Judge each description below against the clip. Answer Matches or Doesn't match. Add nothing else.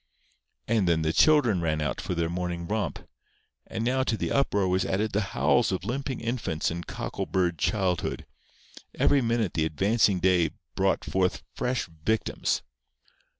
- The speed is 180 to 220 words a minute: Doesn't match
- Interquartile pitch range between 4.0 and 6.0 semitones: Matches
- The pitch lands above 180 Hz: Doesn't match